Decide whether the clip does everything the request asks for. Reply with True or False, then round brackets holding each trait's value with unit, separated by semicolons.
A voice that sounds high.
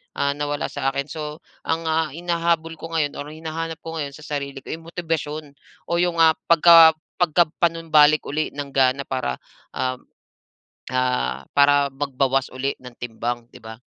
False (150 Hz)